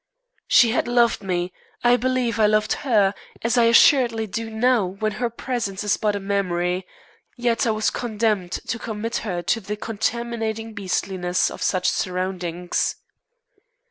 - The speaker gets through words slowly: No, average, 150 wpm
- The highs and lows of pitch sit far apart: No, average, 3.5 semitones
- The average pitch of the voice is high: Yes, high, 215 Hz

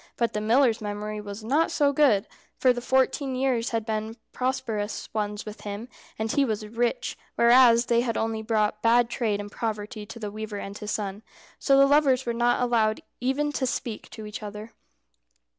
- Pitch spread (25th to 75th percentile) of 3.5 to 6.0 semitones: No, average, 3.1 semitones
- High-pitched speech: Yes, high, 225 Hz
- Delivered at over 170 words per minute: Yes, average, 190 wpm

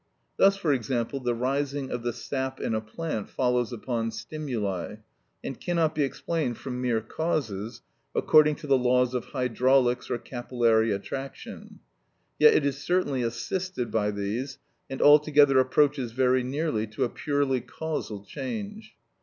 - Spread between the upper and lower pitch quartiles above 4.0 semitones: No, average, 3.7 semitones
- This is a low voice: Yes, low, 130 Hz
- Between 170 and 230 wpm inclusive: No, average, 145 wpm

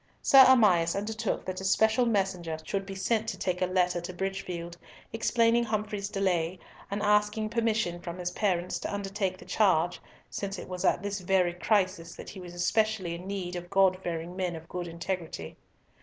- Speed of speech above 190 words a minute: No, average, 185 wpm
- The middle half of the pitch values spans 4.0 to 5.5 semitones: No, average, 2.9 semitones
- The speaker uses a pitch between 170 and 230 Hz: Yes, high, 190 Hz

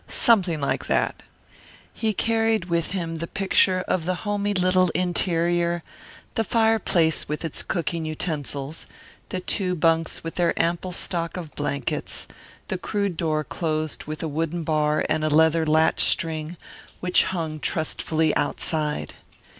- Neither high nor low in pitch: Yes, medium, 165 Hz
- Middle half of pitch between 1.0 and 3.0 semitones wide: Yes, average, 2.7 semitones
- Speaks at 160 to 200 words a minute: No, average, 140 wpm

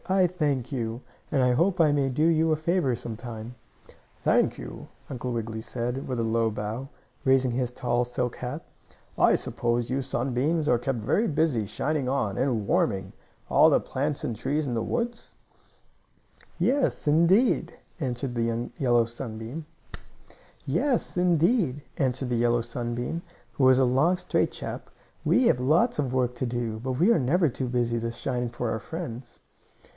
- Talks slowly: No, average, 155 wpm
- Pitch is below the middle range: Yes, low, 125 Hz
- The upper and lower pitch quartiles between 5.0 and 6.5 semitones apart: No, average, 4.3 semitones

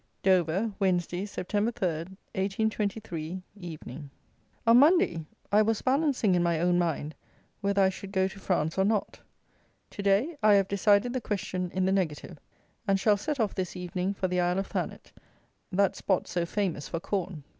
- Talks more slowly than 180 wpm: Yes, average, 170 wpm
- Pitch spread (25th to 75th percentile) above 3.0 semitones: No, average, 2.7 semitones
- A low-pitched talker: No, high, 190 Hz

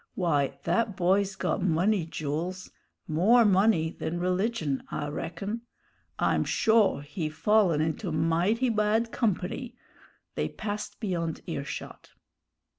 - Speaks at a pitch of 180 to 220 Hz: Yes, medium, 185 Hz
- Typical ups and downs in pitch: Yes, average, 4.8 semitones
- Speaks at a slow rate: Yes, slow, 115 wpm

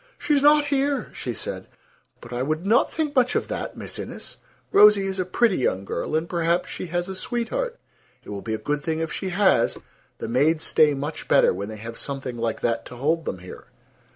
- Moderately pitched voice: Yes, medium, 165 Hz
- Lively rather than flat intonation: Yes, wide, 8.8 semitones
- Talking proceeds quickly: Yes, fast, 215 wpm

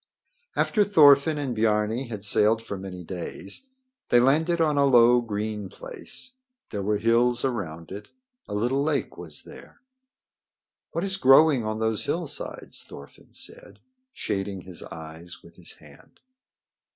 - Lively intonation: Yes, wide, 5.8 semitones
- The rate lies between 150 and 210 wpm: No, average, 140 wpm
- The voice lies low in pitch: Yes, low, 115 Hz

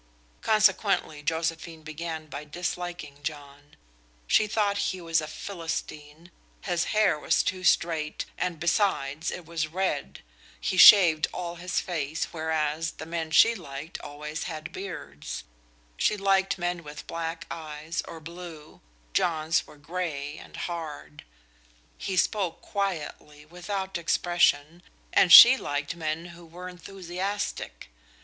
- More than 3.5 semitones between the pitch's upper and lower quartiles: No, average, 2.9 semitones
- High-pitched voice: No, medium, 165 Hz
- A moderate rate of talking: No, slow, 130 wpm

